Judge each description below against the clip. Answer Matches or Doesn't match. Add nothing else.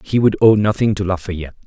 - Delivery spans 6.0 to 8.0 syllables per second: Matches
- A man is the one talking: Matches